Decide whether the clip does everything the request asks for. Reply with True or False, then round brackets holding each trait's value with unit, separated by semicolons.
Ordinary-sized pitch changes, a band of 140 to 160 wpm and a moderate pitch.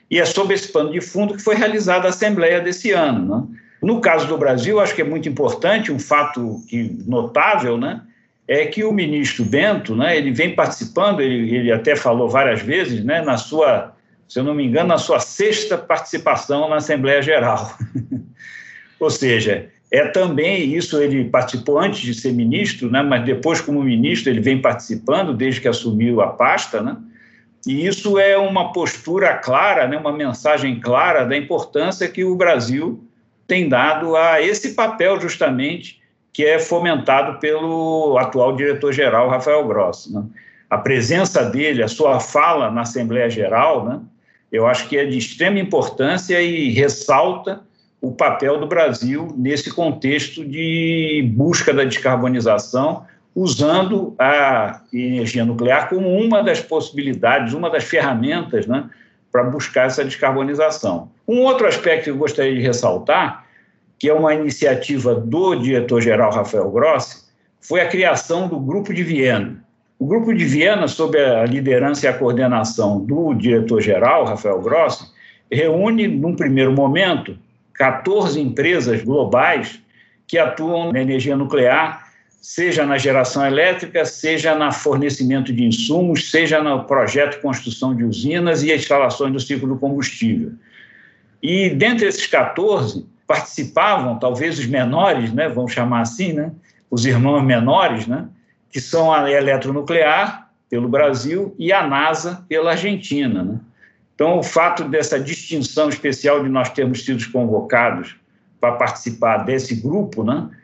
True (4.9 semitones; 150 wpm; 145 Hz)